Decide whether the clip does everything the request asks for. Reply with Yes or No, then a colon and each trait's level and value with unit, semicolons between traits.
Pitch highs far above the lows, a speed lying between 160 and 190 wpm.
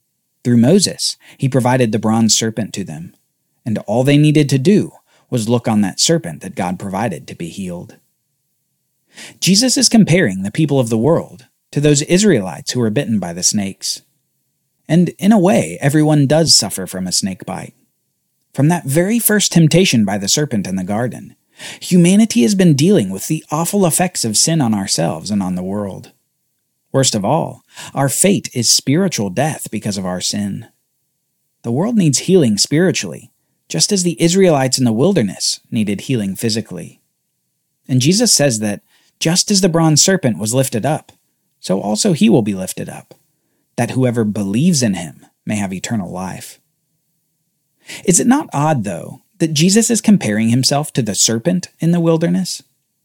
Yes: wide, 7.2 semitones; average, 170 wpm